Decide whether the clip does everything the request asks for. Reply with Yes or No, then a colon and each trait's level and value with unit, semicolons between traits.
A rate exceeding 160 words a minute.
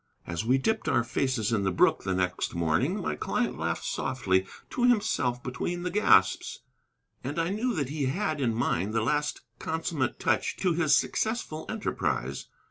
Yes: average, 170 wpm